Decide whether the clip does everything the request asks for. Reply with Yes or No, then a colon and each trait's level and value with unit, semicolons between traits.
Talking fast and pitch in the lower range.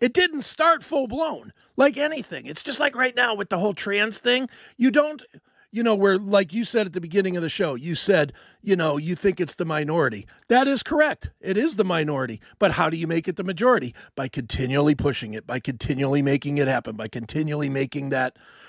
No: fast, 220 wpm; high, 190 Hz